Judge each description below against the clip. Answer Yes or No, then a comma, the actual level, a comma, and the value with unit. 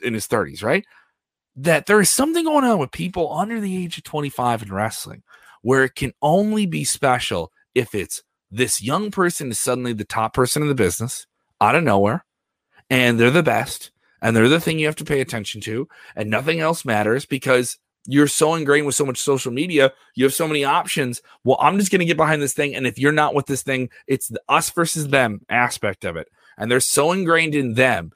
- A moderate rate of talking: No, fast, 220 wpm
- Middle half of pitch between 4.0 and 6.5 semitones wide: Yes, average, 4.7 semitones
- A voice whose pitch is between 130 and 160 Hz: Yes, medium, 140 Hz